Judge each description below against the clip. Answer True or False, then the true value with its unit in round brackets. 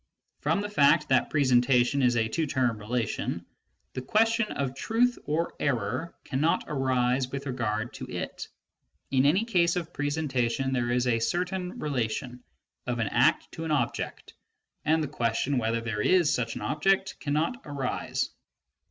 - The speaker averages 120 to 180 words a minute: True (155 wpm)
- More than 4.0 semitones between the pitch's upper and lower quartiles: True (4.8 semitones)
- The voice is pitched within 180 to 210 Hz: False (135 Hz)